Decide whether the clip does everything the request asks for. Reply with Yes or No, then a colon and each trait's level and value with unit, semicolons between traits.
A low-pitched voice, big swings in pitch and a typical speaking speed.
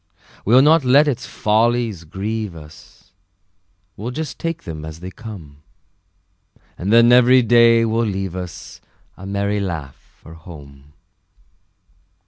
No: low, 105 Hz; wide, 6.1 semitones; slow, 125 wpm